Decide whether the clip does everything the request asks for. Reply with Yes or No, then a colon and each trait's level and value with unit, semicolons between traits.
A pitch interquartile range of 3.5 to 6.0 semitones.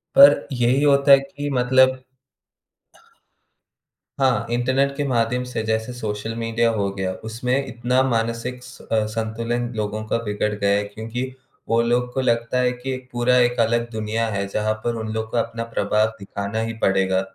No: narrow, 2.4 semitones